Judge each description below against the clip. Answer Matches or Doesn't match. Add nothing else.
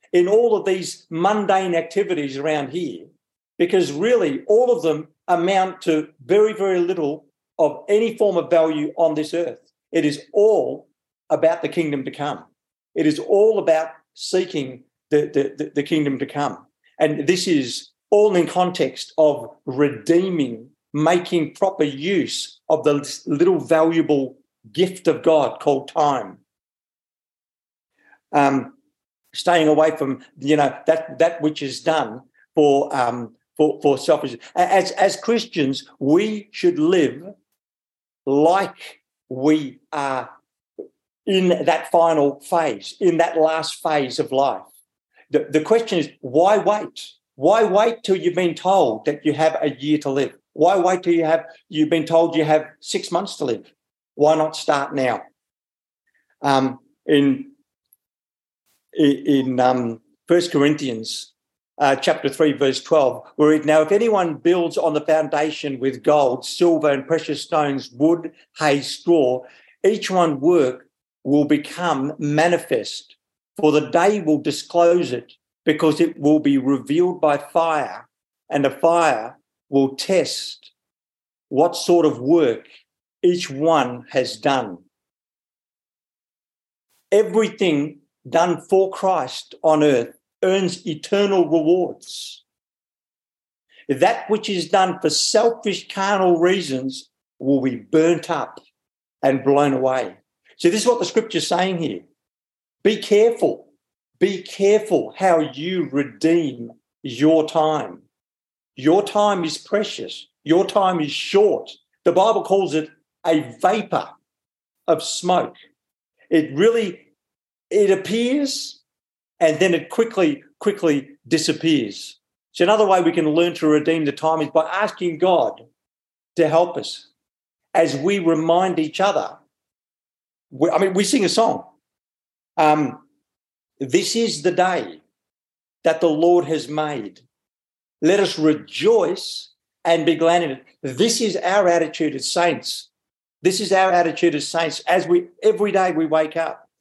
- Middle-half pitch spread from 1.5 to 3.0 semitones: Doesn't match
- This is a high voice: Doesn't match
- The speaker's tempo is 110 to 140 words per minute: Matches